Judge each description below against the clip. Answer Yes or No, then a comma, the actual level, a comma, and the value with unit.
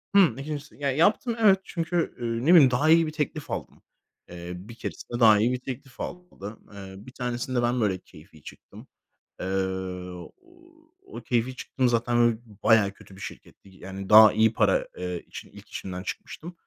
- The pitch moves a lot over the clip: Yes, wide, 6.4 semitones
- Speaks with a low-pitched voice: Yes, low, 120 Hz